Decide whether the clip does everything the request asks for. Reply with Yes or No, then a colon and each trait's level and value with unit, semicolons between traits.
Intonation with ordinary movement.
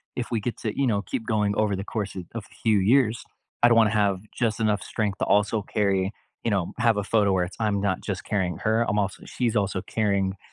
No: narrow, 2.2 semitones